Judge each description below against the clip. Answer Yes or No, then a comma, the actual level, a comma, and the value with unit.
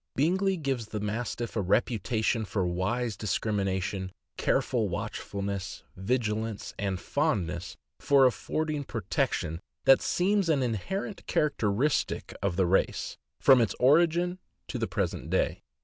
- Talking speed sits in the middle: No, slow, 125 wpm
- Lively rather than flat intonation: Yes, wide, 6.6 semitones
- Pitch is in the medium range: No, low, 115 Hz